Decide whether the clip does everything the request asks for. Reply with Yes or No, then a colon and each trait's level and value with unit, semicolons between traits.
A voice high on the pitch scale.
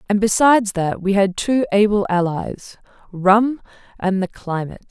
Yes: high, 200 Hz